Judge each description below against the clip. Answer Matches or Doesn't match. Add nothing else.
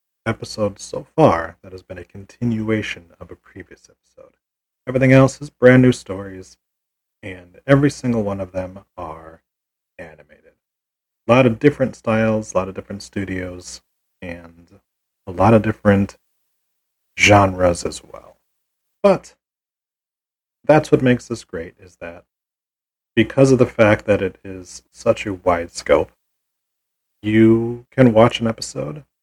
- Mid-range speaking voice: Doesn't match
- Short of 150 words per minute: Matches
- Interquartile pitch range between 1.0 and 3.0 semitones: Doesn't match